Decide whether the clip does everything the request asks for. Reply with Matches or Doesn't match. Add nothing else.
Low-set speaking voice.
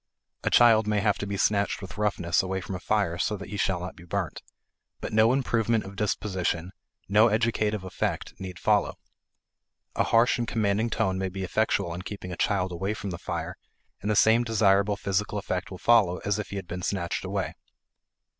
Matches